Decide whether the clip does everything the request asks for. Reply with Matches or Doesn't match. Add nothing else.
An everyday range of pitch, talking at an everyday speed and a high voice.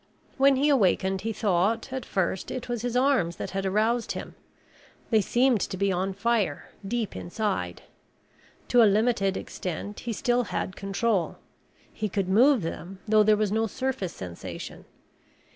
Matches